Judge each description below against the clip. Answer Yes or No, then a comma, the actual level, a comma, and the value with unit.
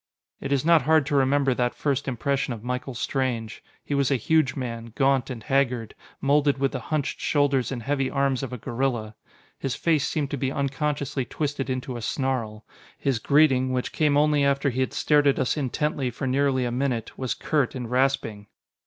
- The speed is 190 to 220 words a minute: Yes, average, 195 wpm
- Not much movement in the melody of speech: Yes, narrow, 2.2 semitones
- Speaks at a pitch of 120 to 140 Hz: Yes, low, 135 Hz